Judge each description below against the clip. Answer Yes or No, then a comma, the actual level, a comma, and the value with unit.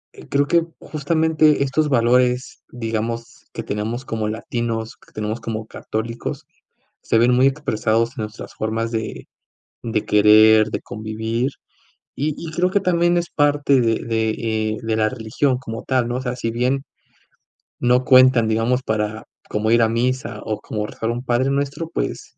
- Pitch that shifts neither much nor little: Yes, average, 3.2 semitones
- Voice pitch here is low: Yes, low, 115 Hz